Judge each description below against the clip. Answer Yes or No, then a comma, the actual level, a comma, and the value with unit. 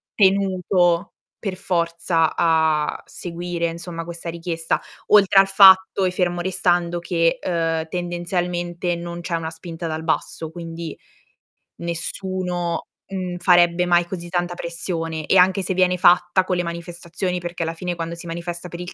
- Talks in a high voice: No, medium, 175 Hz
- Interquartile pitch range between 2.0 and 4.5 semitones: No, narrow, 1.3 semitones